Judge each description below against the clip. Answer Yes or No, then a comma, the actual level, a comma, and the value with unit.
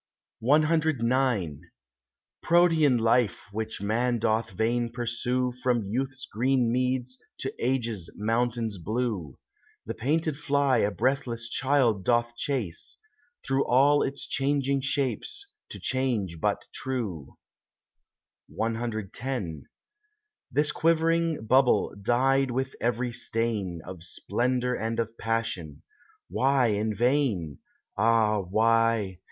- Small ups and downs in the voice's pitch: No, average, 3.3 semitones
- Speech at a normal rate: No, slow, 105 wpm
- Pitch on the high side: No, low, 120 Hz